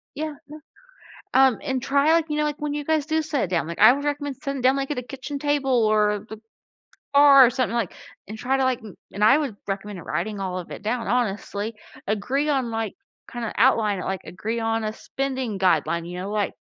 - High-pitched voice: Yes, high, 245 Hz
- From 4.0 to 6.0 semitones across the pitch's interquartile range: Yes, average, 5.1 semitones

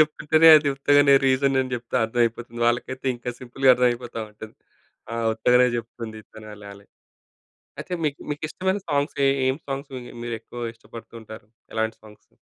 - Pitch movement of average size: Yes, average, 3.5 semitones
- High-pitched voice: No, low, 120 Hz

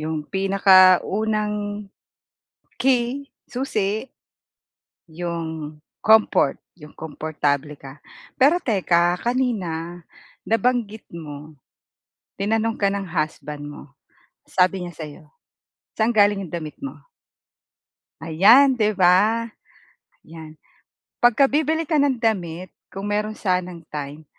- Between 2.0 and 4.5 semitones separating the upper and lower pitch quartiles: No, wide, 5.6 semitones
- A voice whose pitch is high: Yes, high, 195 Hz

